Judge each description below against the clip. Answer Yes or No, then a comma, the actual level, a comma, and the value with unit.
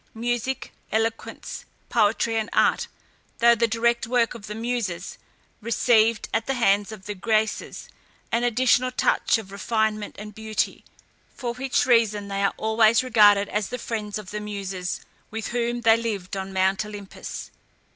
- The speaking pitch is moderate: No, high, 220 Hz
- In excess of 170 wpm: No, average, 155 wpm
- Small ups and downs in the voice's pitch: Yes, narrow, 2.3 semitones